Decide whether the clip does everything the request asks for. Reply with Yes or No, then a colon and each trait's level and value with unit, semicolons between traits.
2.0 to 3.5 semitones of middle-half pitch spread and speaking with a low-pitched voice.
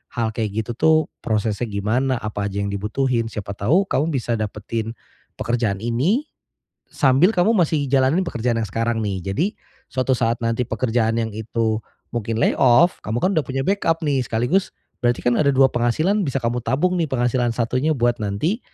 No: average, 4.0 semitones; low, 120 Hz